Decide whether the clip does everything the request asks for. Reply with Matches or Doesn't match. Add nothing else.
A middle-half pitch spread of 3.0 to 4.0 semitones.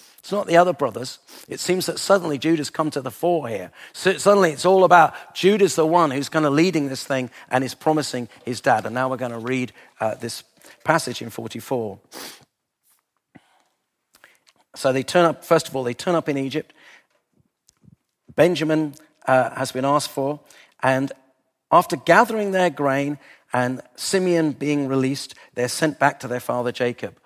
Doesn't match